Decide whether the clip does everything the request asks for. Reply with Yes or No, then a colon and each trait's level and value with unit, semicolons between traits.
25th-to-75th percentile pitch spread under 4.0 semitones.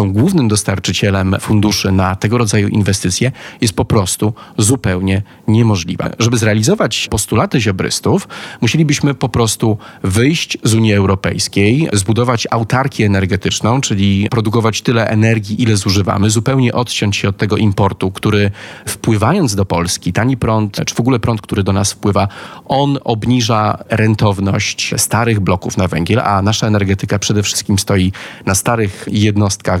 Yes: average, 2.9 semitones